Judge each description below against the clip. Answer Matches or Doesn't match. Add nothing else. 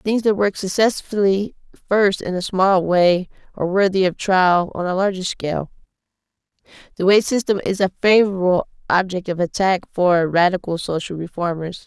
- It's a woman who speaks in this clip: Matches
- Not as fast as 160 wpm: Matches